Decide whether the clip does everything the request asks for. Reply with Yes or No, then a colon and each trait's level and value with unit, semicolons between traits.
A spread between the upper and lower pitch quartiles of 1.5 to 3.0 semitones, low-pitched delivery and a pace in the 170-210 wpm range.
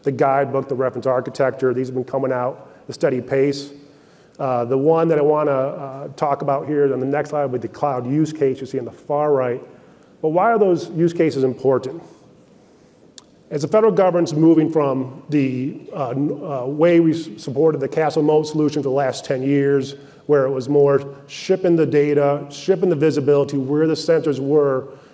No: narrow, 2.4 semitones; medium, 145 Hz; average, 200 wpm